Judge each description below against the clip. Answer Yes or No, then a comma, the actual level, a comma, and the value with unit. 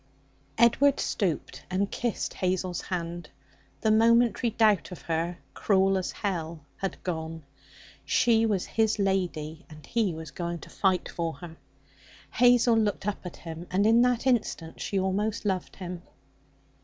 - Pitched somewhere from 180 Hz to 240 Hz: Yes, high, 190 Hz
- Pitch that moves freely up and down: No, average, 4.4 semitones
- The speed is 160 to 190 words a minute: No, average, 145 wpm